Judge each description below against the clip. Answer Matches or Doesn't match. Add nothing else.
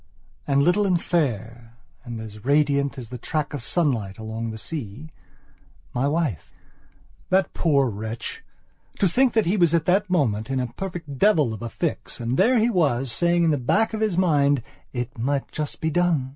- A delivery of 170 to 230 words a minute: Matches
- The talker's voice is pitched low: Doesn't match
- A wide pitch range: Matches